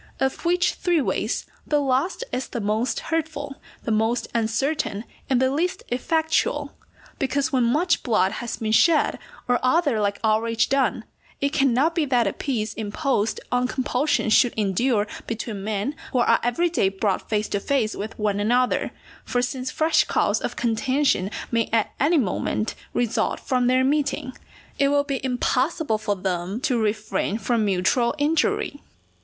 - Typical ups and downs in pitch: Yes, average, 4.6 semitones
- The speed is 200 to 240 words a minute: No, average, 160 wpm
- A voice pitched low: No, high, 245 Hz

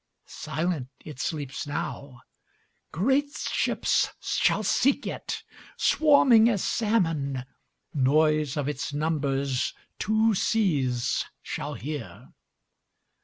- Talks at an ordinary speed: No, slow, 75 wpm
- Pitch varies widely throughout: Yes, wide, 7.7 semitones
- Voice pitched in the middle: Yes, medium, 155 Hz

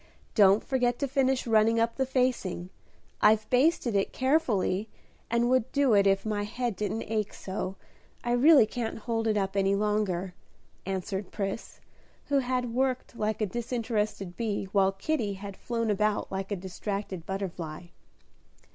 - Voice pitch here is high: Yes, high, 215 Hz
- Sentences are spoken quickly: No, average, 155 wpm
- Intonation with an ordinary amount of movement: Yes, average, 3.7 semitones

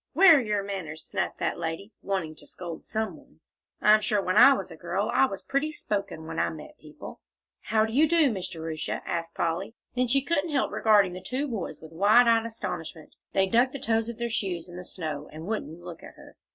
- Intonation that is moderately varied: No, wide, 5.9 semitones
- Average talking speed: No, fast, 225 wpm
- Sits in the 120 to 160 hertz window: No, high, 205 Hz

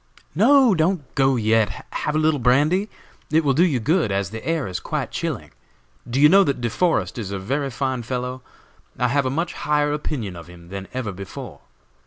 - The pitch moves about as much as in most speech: No, wide, 5.8 semitones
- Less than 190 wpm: No, fast, 205 wpm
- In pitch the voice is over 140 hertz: No, low, 135 Hz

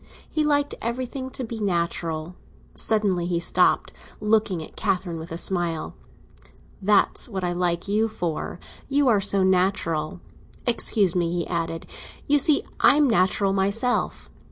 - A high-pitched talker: Yes, high, 195 Hz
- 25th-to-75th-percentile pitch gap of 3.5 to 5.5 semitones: Yes, average, 4.6 semitones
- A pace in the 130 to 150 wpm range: Yes, average, 145 wpm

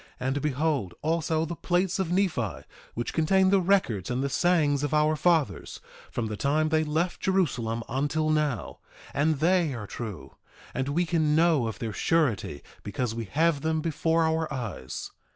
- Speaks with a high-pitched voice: No, medium, 150 Hz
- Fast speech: No, average, 170 wpm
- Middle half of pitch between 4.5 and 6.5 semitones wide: Yes, average, 5.0 semitones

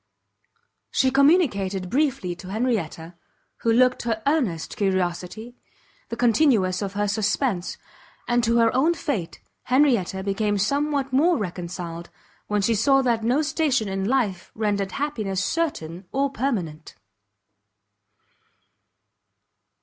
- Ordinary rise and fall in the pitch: No, wide, 6.0 semitones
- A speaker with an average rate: No, slow, 115 wpm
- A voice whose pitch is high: Yes, high, 225 Hz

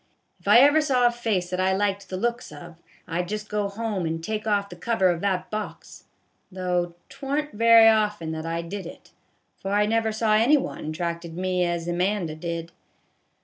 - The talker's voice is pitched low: No, high, 195 Hz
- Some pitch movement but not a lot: Yes, average, 4.2 semitones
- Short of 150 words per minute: No, fast, 205 wpm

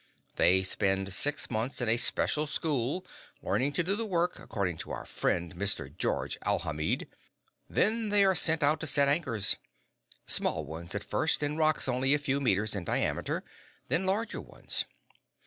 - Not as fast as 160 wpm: No, average, 165 wpm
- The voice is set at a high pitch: No, medium, 140 Hz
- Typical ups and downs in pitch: No, wide, 8.4 semitones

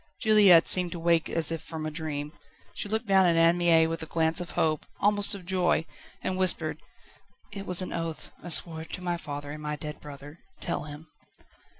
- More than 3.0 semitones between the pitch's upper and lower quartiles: No, average, 2.7 semitones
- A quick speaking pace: Yes, fast, 210 wpm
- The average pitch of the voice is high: No, medium, 165 Hz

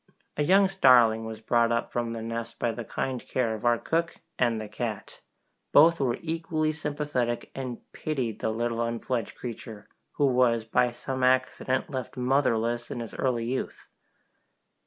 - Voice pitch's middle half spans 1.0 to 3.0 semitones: Yes, narrow, 2.5 semitones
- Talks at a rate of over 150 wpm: Yes, average, 160 wpm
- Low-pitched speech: Yes, low, 120 Hz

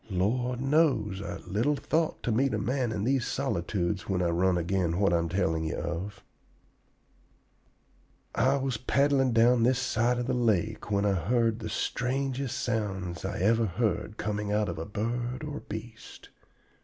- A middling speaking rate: Yes, average, 170 wpm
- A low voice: Yes, low, 110 Hz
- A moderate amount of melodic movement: Yes, average, 4.5 semitones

